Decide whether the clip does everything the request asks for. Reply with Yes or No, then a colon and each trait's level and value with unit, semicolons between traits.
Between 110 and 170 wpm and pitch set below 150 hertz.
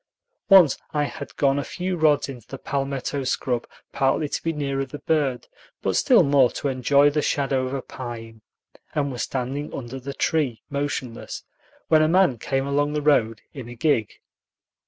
No: average, 180 wpm; medium, 140 Hz